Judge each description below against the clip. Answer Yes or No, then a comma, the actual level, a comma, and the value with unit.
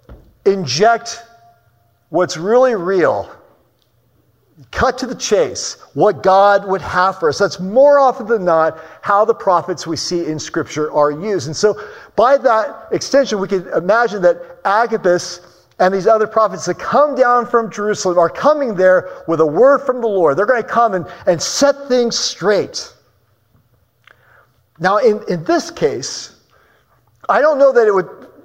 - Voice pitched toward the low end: No, high, 200 Hz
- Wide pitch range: Yes, wide, 5.7 semitones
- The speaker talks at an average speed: Yes, average, 160 wpm